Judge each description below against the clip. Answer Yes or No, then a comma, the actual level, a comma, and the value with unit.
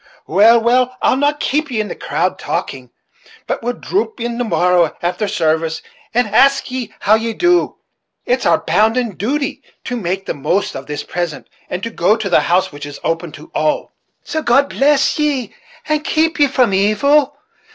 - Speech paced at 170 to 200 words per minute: Yes, average, 185 wpm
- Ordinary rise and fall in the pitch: No, wide, 7.2 semitones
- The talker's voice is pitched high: Yes, high, 230 Hz